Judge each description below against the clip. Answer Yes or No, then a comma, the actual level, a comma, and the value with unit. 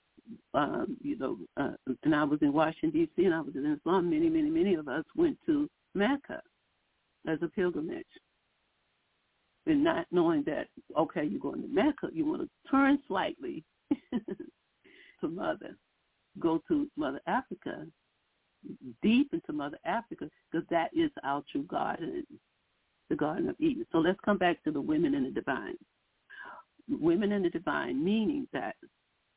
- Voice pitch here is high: Yes, very high, 305 Hz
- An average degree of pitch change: No, wide, 8.0 semitones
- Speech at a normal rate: Yes, average, 155 wpm